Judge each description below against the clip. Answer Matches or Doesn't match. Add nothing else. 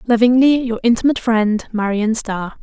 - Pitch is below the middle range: Doesn't match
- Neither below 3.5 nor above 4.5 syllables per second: Doesn't match